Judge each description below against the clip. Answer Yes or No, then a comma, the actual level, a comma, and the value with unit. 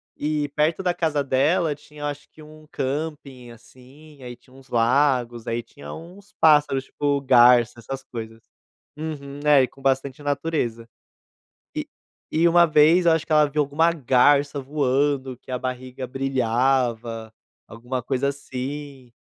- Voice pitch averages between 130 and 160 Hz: Yes, medium, 140 Hz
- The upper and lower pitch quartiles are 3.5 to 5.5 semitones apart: No, average, 3.0 semitones